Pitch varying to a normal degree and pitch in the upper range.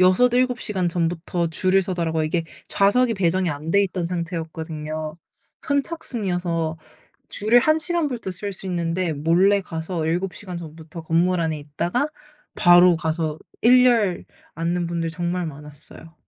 No: average, 3.2 semitones; medium, 175 Hz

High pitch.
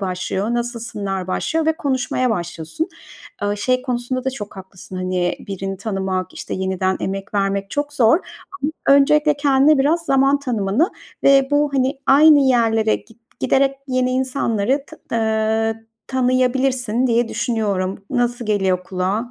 Yes: high, 235 Hz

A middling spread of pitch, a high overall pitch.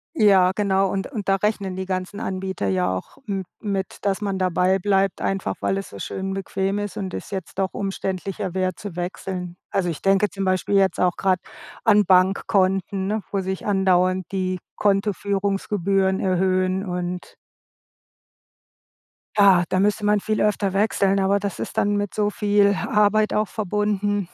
No: narrow, 1.5 semitones; high, 195 Hz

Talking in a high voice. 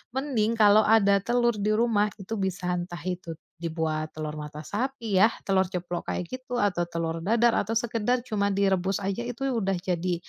Yes: high, 200 Hz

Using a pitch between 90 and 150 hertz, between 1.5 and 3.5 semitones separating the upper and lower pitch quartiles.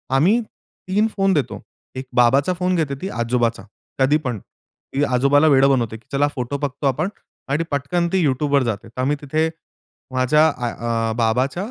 No: medium, 140 Hz; average, 3.9 semitones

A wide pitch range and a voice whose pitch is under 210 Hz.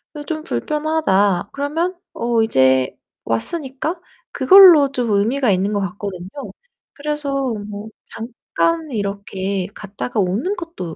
No: wide, 7.2 semitones; high, 235 Hz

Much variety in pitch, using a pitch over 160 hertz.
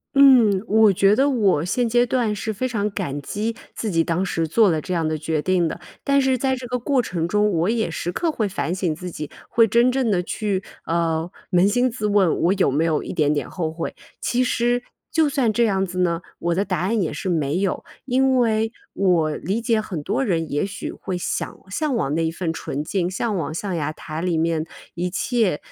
Yes: wide, 5.8 semitones; high, 190 Hz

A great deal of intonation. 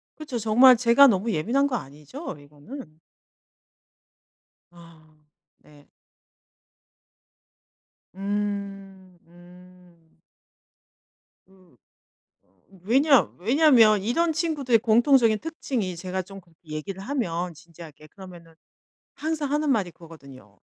Yes: wide, 6.9 semitones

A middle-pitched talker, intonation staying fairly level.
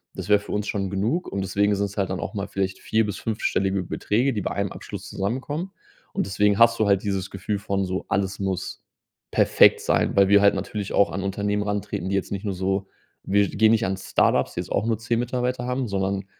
No: low, 100 Hz; narrow, 2.0 semitones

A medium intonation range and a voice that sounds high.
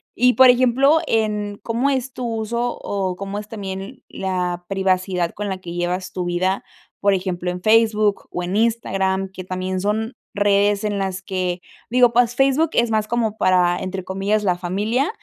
Yes: average, 3.5 semitones; high, 200 Hz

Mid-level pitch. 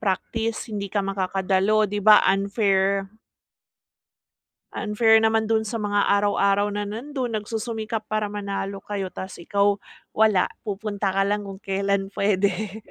No: high, 205 Hz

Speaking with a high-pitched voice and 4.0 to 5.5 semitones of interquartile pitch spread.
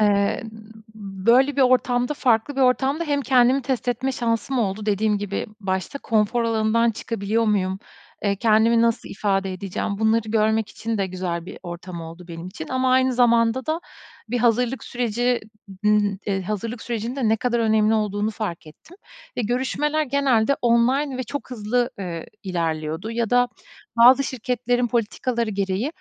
No: high, 230 Hz; average, 3.3 semitones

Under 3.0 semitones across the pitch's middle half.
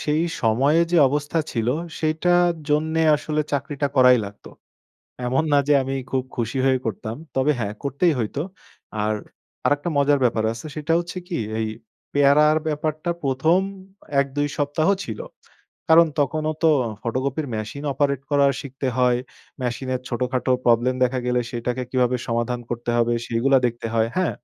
No: average, 3.7 semitones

